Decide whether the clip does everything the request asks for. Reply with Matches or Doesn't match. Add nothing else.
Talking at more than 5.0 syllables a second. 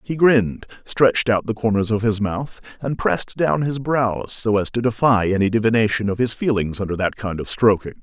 Matches